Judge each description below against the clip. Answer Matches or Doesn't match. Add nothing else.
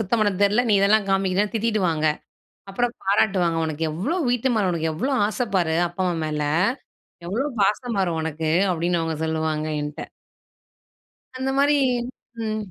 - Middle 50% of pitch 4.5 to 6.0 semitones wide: Matches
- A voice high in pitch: Matches